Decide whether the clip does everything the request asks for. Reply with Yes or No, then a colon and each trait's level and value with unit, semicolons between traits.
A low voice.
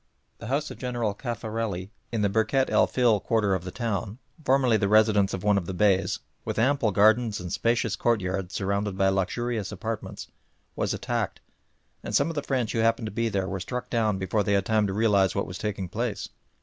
Yes: low, 105 Hz